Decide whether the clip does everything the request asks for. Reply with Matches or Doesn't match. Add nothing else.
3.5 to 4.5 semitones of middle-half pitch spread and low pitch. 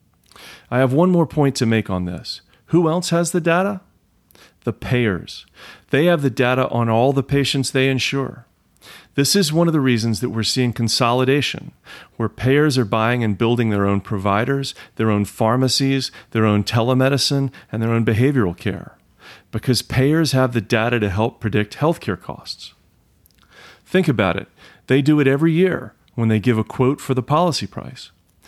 Matches